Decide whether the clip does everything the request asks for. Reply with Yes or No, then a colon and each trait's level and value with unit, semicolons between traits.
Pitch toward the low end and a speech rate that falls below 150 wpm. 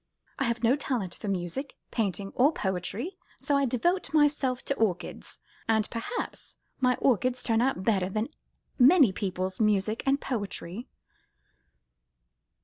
No: high, 230 Hz; slow, 135 wpm